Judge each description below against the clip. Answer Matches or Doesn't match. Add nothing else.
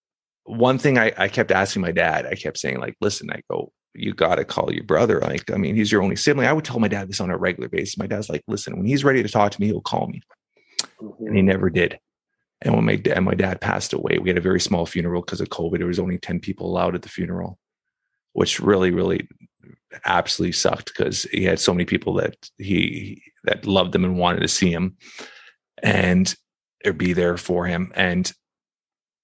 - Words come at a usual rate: Doesn't match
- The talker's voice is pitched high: Doesn't match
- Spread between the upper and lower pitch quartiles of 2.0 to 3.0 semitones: Doesn't match